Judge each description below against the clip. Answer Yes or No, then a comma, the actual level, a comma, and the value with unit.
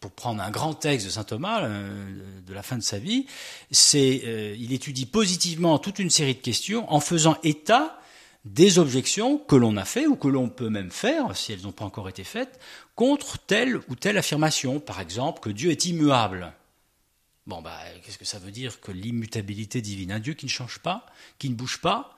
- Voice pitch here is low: Yes, low, 130 Hz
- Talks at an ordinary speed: Yes, average, 210 wpm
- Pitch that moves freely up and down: Yes, wide, 7.3 semitones